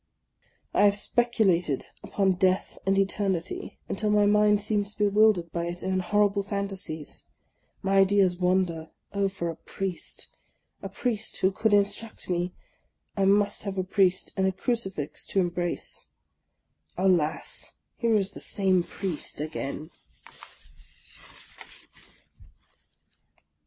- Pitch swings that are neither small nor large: No, narrow, 2.3 semitones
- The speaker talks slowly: Yes, slow, 120 wpm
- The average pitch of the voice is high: Yes, high, 195 Hz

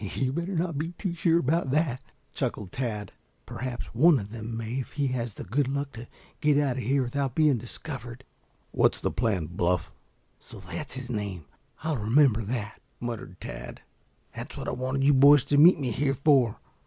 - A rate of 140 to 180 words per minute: No, average, 190 wpm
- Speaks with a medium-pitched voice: No, low, 130 Hz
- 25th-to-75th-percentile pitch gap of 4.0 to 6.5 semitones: Yes, average, 4.3 semitones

